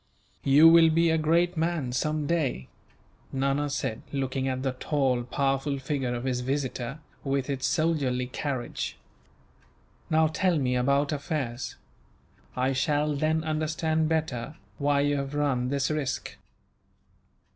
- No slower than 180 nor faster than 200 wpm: No, slow, 135 wpm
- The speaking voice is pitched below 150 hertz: Yes, medium, 140 Hz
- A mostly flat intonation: No, average, 3.0 semitones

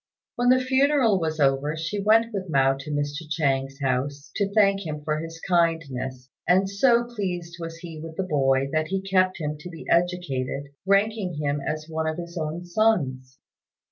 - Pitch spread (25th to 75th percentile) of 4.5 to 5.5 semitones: Yes, average, 5.0 semitones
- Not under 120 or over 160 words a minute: No, average, 180 wpm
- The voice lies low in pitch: No, medium, 165 Hz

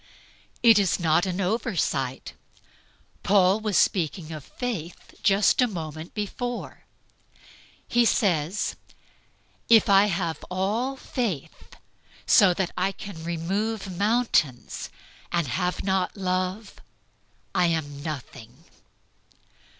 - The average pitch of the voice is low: No, medium, 185 Hz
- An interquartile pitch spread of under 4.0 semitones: No, average, 4.3 semitones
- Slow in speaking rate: Yes, slow, 105 wpm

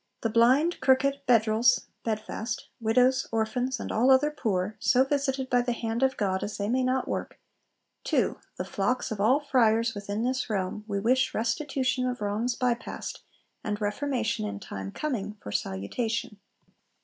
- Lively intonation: No, average, 3.6 semitones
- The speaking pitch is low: No, high, 235 Hz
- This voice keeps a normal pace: Yes, average, 160 wpm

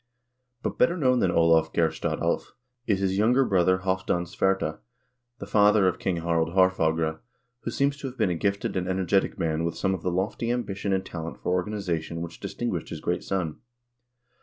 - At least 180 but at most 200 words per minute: Yes, average, 185 wpm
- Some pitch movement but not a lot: Yes, average, 3.3 semitones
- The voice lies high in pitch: No, very low, 95 Hz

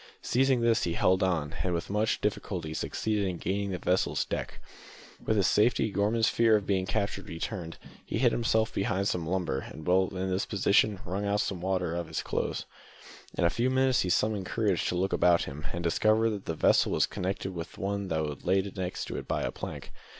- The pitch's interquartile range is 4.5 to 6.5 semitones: No, average, 3.4 semitones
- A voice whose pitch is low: Yes, very low, 95 Hz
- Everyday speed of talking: No, fast, 215 wpm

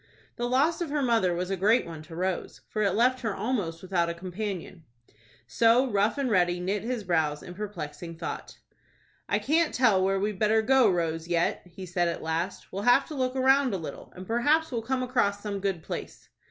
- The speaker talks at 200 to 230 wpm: Yes, fast, 205 wpm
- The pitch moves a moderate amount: No, wide, 5.8 semitones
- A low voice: No, high, 200 Hz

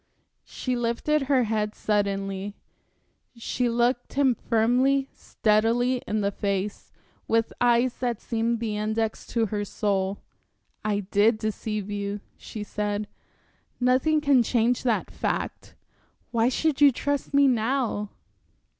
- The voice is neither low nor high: No, high, 230 Hz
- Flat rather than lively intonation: No, average, 3.1 semitones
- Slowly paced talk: Yes, slow, 125 wpm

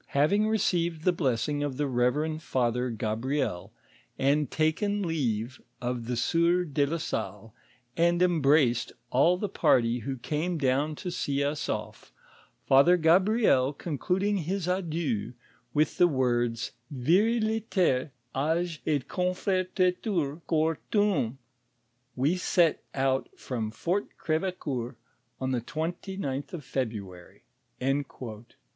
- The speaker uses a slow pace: Yes, slow, 120 wpm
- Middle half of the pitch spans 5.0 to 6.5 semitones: Yes, wide, 5.6 semitones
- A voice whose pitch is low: No, medium, 150 Hz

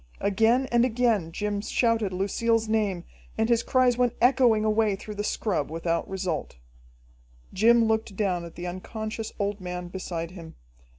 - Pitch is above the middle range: Yes, high, 210 Hz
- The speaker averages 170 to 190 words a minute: No, average, 155 wpm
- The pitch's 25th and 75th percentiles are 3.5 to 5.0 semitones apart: Yes, average, 3.8 semitones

